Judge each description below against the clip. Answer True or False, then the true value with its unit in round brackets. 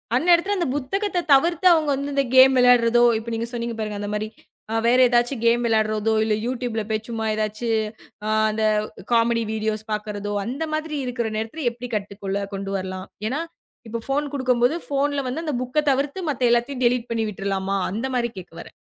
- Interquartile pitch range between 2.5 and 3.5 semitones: False (4.0 semitones)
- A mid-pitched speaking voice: False (235 Hz)